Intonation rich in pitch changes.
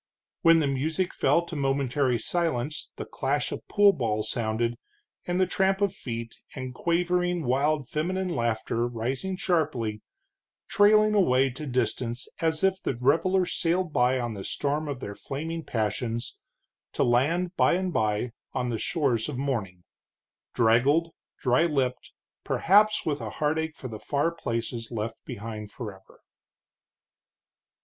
Yes: wide, 6.2 semitones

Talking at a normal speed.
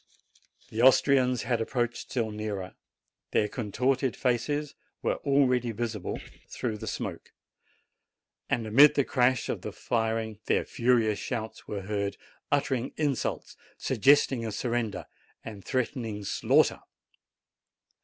No: slow, 120 wpm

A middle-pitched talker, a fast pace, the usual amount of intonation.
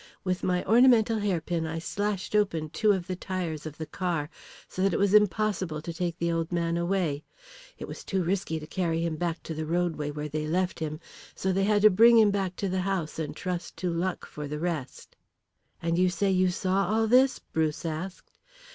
Yes: medium, 180 Hz; fast, 210 wpm; average, 3.2 semitones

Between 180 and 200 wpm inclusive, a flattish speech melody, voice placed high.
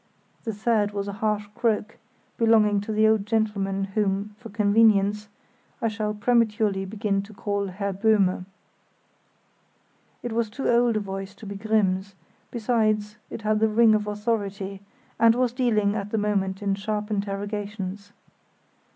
No: average, 150 wpm; narrow, 1.7 semitones; high, 210 Hz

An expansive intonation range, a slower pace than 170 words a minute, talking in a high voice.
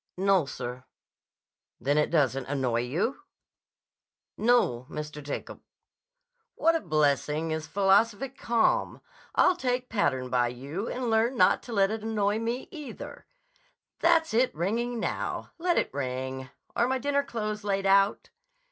Yes: wide, 8.8 semitones; average, 140 wpm; high, 195 Hz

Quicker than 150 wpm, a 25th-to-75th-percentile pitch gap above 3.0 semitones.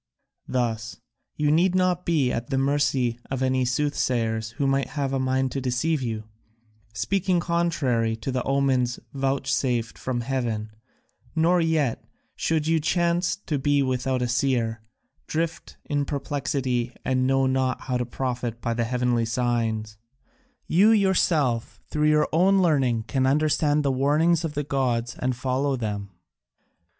No: average, 145 wpm; average, 3.7 semitones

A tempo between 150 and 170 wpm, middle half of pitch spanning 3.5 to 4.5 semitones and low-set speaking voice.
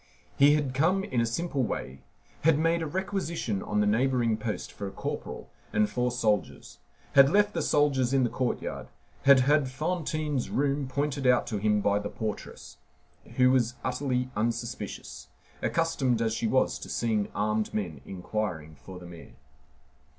No: average, 165 wpm; average, 5.2 semitones; low, 125 Hz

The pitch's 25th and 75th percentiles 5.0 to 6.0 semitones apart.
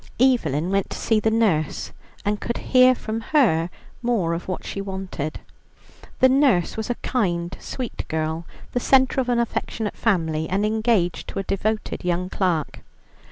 Yes: wide, 5.5 semitones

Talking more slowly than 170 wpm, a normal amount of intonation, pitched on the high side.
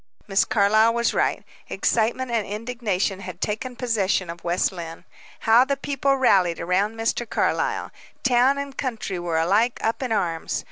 Yes: average, 155 wpm; average, 4.8 semitones; high, 220 Hz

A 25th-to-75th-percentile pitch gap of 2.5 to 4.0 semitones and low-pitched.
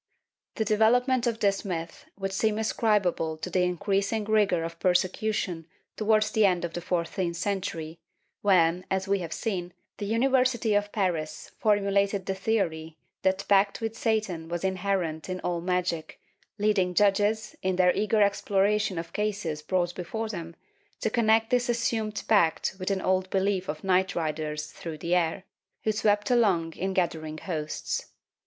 No: average, 3.6 semitones; high, 190 Hz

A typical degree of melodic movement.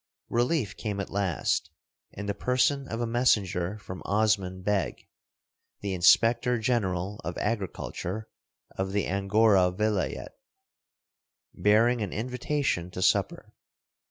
Yes: average, 3.7 semitones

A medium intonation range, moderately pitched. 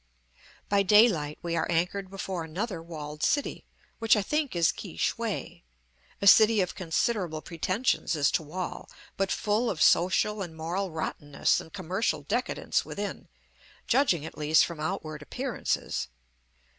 Yes: average, 4.6 semitones; medium, 180 Hz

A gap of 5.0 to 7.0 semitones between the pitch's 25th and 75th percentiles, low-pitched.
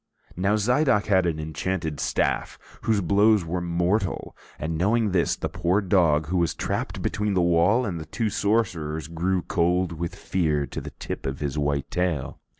No: average, 4.0 semitones; very low, 90 Hz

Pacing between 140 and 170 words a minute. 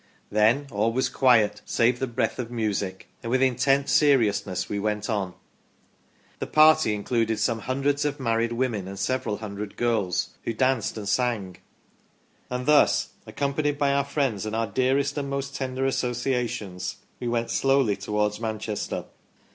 Yes: average, 165 wpm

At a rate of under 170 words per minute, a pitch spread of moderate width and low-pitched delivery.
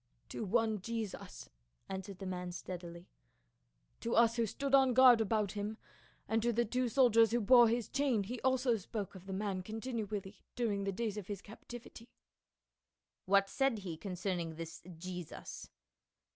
No: average, 160 wpm; average, 3.7 semitones; high, 215 Hz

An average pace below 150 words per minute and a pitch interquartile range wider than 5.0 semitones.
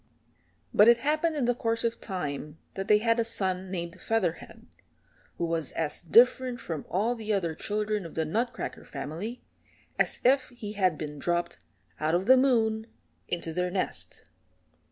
No: average, 165 wpm; wide, 5.4 semitones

